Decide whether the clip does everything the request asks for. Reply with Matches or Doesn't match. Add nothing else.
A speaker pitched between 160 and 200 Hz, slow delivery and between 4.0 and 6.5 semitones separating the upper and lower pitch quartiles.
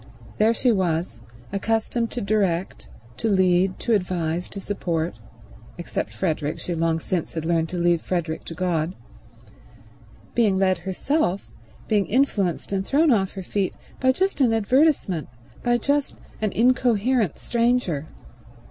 Matches